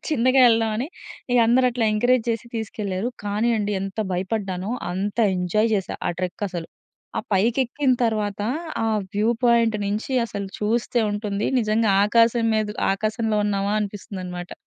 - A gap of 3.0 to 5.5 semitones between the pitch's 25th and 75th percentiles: No, narrow, 2.5 semitones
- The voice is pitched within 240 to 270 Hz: No, high, 215 Hz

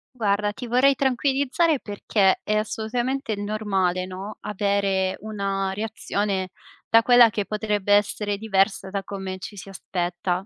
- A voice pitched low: No, high, 205 Hz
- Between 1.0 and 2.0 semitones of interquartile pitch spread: No, narrow, 2.4 semitones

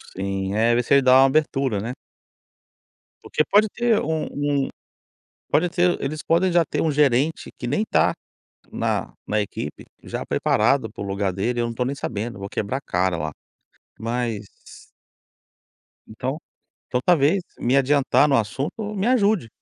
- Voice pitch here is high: No, low, 135 Hz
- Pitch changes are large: Yes, wide, 5.9 semitones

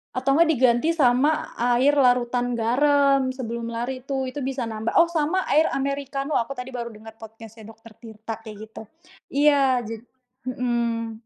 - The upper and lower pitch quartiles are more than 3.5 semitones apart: No, average, 3.2 semitones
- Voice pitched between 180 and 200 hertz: No, very high, 250 Hz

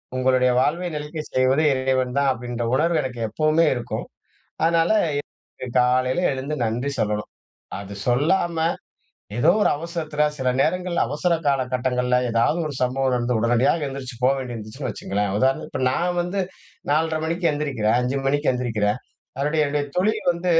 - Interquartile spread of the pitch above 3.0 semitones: Yes, average, 4.1 semitones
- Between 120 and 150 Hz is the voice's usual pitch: Yes, low, 135 Hz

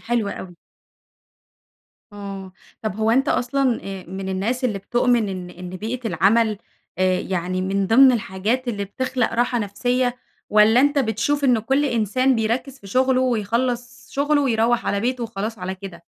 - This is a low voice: No, high, 225 Hz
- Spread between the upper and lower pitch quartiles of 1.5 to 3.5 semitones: No, average, 4.3 semitones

